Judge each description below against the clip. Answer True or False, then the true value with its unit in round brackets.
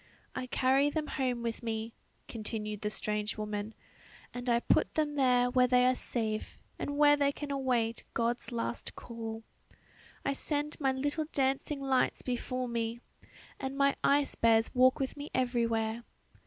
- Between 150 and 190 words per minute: True (155 wpm)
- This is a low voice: False (250 Hz)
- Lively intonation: False (3.2 semitones)